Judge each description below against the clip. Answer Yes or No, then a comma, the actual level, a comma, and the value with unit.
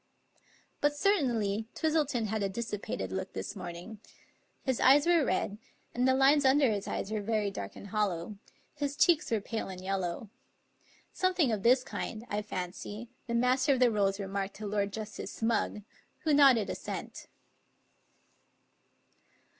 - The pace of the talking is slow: No, average, 155 wpm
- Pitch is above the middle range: Yes, high, 220 Hz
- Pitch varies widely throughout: No, average, 4.9 semitones